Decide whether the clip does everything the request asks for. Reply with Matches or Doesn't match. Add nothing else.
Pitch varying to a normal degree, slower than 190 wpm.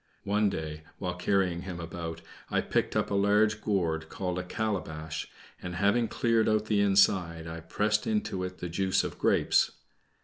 Matches